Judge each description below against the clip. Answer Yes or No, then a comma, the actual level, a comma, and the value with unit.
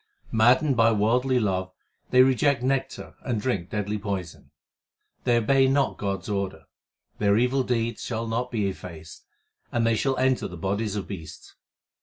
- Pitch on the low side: Yes, low, 115 Hz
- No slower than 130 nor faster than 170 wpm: Yes, average, 160 wpm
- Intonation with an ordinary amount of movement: Yes, average, 4.3 semitones